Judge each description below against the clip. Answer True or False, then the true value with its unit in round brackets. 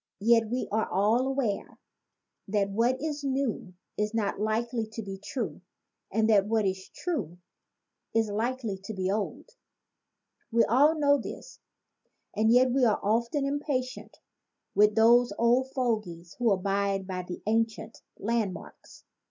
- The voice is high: True (225 Hz)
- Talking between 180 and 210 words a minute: False (145 wpm)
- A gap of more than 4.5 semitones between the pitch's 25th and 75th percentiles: False (3.8 semitones)